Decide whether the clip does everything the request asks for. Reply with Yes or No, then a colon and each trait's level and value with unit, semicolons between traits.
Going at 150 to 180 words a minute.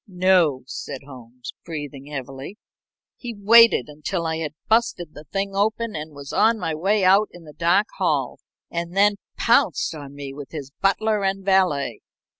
Yes: average, 165 wpm